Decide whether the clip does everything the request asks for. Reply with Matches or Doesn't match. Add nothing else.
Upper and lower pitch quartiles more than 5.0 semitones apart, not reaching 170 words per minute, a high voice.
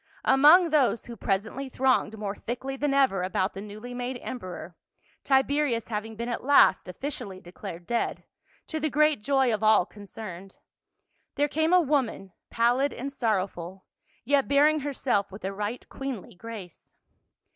Matches